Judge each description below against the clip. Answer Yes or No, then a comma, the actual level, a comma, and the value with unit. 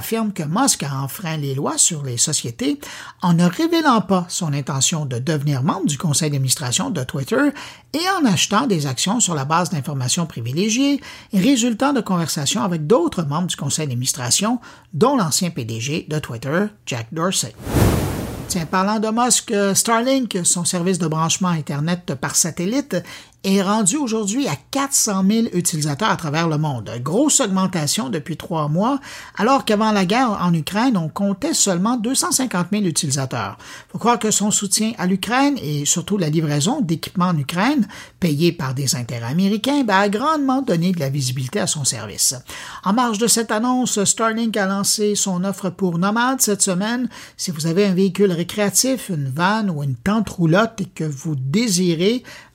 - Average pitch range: No, wide, 6.0 semitones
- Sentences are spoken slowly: No, average, 170 wpm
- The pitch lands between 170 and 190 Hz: Yes, medium, 185 Hz